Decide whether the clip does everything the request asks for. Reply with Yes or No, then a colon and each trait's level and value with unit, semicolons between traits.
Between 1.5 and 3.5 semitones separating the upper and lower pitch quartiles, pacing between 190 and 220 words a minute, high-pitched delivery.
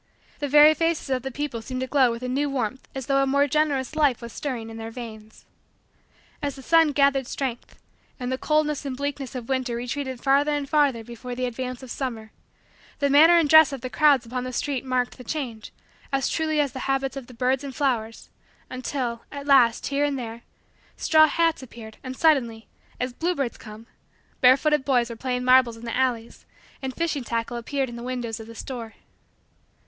Yes: average, 3.1 semitones; average, 200 wpm; very high, 260 Hz